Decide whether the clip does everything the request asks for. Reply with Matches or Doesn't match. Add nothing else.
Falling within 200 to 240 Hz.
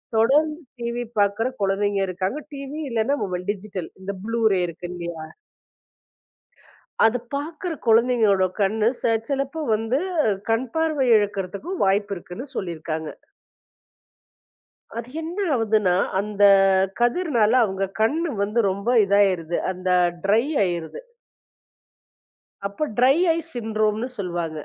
Matches